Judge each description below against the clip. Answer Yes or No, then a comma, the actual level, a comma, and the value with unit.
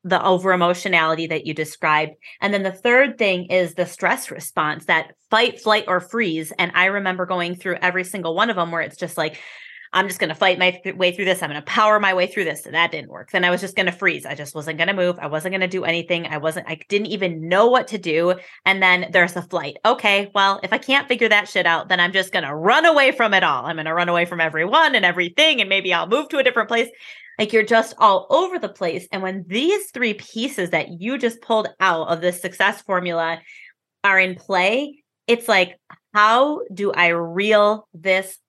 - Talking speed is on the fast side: Yes, fast, 245 wpm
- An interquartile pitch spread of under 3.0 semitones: No, average, 3.7 semitones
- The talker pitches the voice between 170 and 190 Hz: Yes, medium, 185 Hz